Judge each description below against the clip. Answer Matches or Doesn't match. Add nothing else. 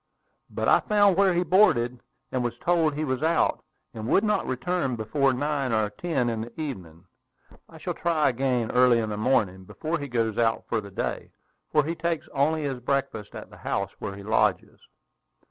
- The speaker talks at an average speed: Matches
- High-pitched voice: Doesn't match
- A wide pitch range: Matches